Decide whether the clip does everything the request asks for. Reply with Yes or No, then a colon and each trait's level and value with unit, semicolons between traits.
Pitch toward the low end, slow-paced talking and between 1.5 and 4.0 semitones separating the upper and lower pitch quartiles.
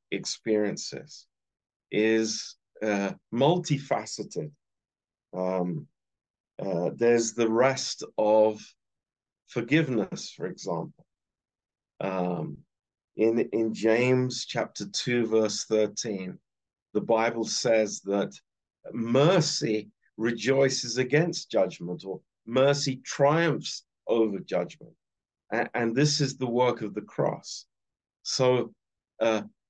Yes: low, 115 Hz; slow, 90 wpm; average, 3.7 semitones